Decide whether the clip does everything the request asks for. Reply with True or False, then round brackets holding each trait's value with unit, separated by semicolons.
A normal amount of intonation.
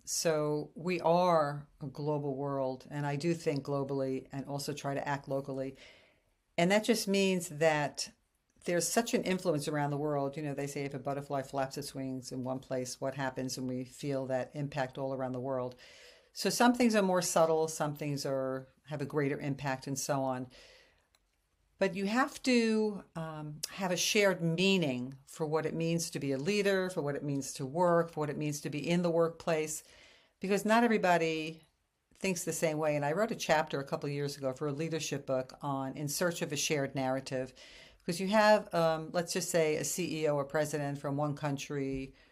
True (3.8 semitones)